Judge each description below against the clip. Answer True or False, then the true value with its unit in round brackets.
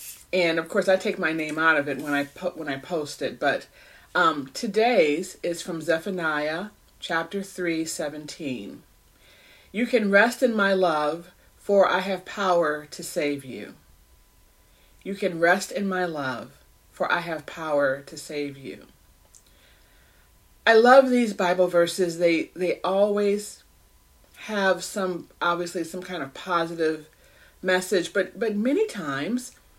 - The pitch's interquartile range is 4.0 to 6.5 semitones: True (4.9 semitones)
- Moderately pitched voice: True (175 Hz)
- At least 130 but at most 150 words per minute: True (145 wpm)